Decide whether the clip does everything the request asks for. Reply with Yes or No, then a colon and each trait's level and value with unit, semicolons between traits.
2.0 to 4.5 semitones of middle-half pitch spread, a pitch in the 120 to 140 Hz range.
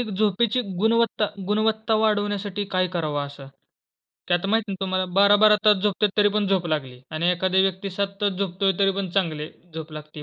No: average, 2.9 semitones; high, 195 Hz